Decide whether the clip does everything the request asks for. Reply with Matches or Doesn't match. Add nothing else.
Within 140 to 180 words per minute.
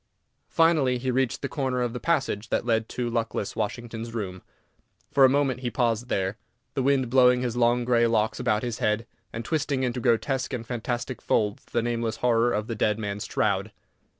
Doesn't match